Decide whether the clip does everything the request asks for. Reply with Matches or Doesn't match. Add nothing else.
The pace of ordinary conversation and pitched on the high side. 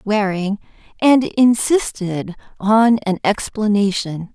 Doesn't match